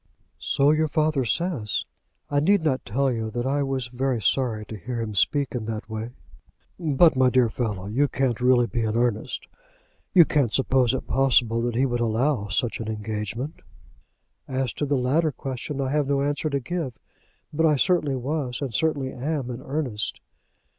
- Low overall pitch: Yes, low, 130 Hz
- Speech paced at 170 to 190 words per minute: Yes, average, 180 wpm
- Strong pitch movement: No, average, 3.6 semitones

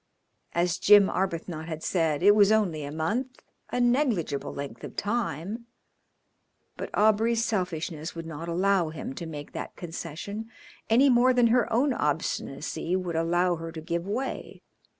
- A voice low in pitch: No, medium, 180 Hz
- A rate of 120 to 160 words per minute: Yes, average, 150 wpm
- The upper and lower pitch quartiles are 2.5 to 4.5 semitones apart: No, wide, 5.4 semitones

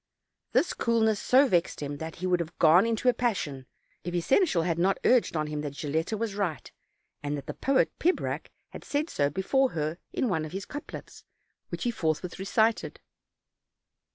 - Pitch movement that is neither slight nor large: No, wide, 6.6 semitones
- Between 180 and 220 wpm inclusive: Yes, average, 195 wpm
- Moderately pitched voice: Yes, medium, 180 Hz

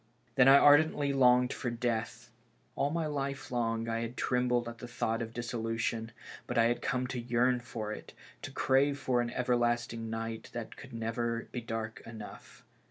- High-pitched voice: No, low, 120 Hz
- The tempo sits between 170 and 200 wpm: Yes, average, 175 wpm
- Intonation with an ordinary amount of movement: No, narrow, 1.8 semitones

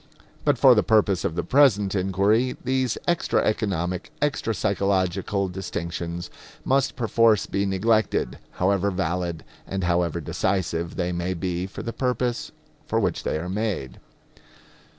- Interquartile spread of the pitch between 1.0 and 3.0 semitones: No, average, 3.8 semitones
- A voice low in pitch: Yes, very low, 95 Hz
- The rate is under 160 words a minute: Yes, slow, 135 wpm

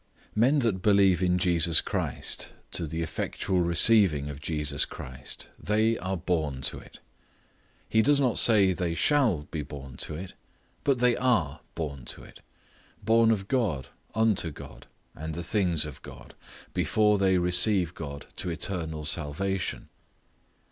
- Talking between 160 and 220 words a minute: No, average, 150 wpm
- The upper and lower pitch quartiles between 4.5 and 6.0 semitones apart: Yes, wide, 5.4 semitones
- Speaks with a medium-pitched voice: No, very low, 90 Hz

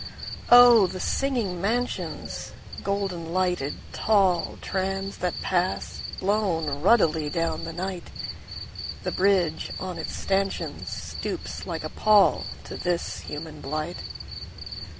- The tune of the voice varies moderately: Yes, average, 3.1 semitones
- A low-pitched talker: No, medium, 185 Hz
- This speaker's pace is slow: Yes, slow, 90 wpm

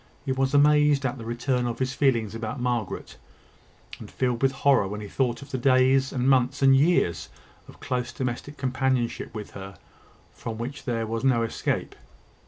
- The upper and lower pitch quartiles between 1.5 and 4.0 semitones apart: Yes, narrow, 2.6 semitones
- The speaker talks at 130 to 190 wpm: Yes, average, 180 wpm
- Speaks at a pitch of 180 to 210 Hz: No, low, 130 Hz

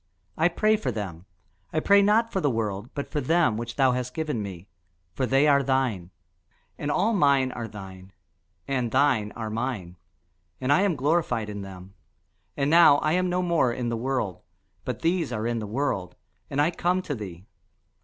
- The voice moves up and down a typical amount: No, wide, 6.6 semitones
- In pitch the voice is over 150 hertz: No, low, 130 Hz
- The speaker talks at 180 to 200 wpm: Yes, average, 190 wpm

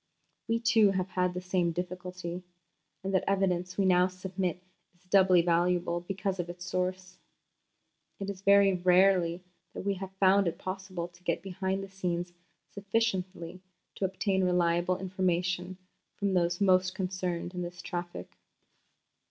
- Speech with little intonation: Yes, narrow, 1.4 semitones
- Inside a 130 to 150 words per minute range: Yes, average, 145 wpm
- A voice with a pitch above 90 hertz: Yes, medium, 185 Hz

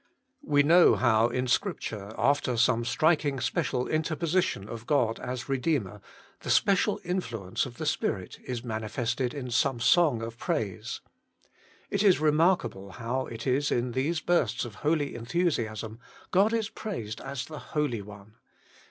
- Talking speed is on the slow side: No, average, 145 wpm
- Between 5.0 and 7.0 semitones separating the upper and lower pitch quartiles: Yes, average, 5.3 semitones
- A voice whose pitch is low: Yes, low, 130 Hz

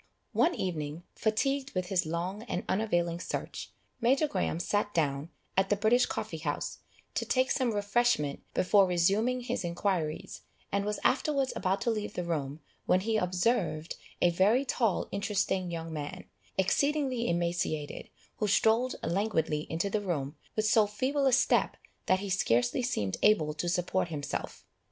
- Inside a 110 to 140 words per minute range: No, average, 155 wpm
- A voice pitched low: No, high, 190 Hz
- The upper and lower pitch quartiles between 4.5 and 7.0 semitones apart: Yes, average, 5.1 semitones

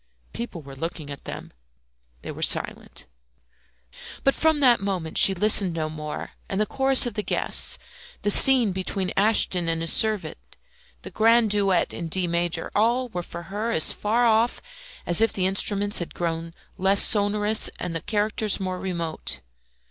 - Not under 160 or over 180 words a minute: Yes, average, 165 wpm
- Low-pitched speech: No, high, 195 Hz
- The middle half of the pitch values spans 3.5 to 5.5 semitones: Yes, average, 4.3 semitones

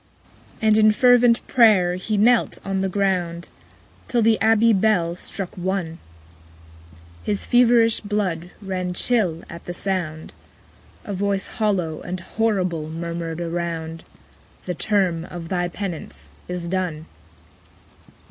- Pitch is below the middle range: No, medium, 185 Hz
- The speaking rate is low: Yes, slow, 130 wpm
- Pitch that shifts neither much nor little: Yes, average, 3.8 semitones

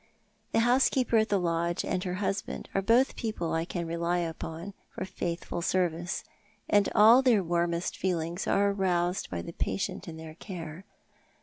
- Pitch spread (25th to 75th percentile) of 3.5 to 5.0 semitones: No, average, 3.1 semitones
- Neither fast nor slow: Yes, average, 165 wpm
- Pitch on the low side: No, medium, 180 Hz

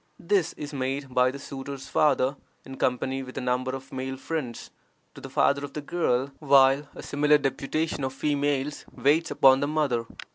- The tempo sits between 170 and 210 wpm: Yes, average, 180 wpm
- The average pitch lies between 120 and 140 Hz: Yes, low, 135 Hz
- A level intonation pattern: Yes, narrow, 1.8 semitones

